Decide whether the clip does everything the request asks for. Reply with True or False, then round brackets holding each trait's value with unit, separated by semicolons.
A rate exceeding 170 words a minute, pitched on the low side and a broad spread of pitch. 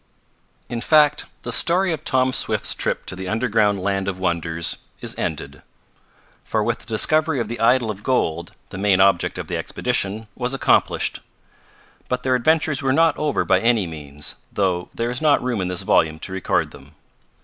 True (180 wpm; 110 Hz; 5.9 semitones)